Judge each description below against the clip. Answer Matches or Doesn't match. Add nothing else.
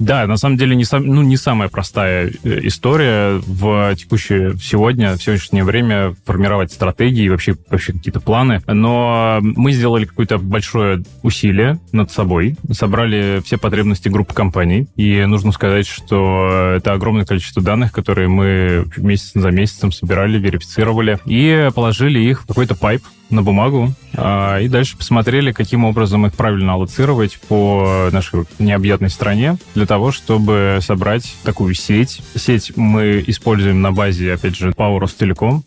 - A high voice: Doesn't match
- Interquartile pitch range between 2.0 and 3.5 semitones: Matches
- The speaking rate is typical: Matches